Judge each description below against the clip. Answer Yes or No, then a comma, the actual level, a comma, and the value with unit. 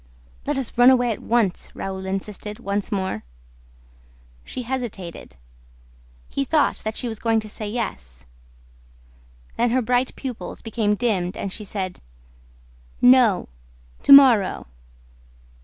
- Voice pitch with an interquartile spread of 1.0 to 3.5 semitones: No, average, 4.1 semitones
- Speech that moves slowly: Yes, slow, 125 wpm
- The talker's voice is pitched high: Yes, high, 220 Hz